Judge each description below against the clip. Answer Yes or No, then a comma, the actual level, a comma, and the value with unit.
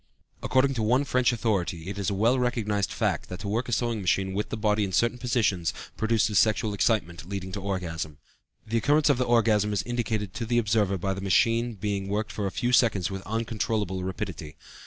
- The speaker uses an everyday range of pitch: Yes, average, 3.2 semitones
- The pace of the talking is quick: Yes, fast, 215 wpm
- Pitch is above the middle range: No, low, 105 Hz